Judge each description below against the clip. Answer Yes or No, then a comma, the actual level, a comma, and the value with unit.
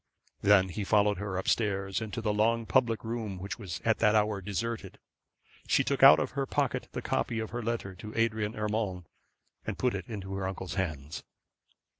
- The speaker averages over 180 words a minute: Yes, average, 195 wpm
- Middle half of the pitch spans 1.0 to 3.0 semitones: Yes, narrow, 2.6 semitones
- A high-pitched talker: No, low, 105 Hz